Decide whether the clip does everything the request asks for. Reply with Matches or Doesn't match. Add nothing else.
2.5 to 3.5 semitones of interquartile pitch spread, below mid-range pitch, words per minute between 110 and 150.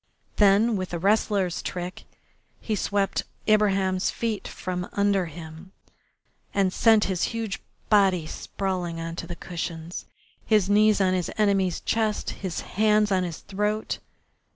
Doesn't match